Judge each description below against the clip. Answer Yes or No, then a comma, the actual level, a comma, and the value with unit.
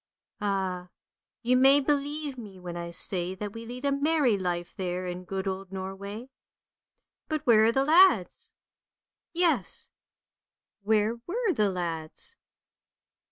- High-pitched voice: Yes, high, 210 Hz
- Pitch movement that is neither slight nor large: No, wide, 6.9 semitones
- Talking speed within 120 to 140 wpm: Yes, slow, 135 wpm